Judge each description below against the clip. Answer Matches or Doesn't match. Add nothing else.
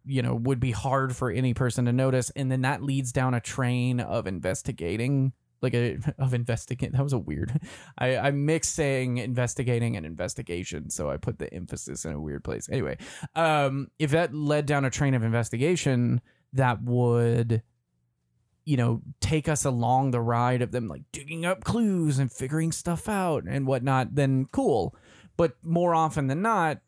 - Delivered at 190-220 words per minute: Doesn't match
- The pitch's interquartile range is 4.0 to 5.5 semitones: Doesn't match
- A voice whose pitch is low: Matches